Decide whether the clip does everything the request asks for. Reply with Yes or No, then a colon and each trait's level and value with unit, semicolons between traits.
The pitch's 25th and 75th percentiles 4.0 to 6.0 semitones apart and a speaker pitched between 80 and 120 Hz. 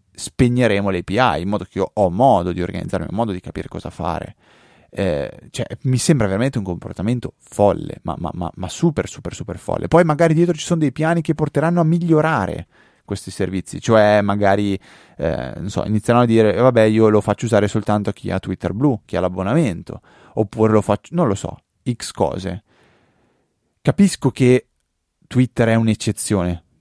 Yes: average, 5.1 semitones; low, 110 Hz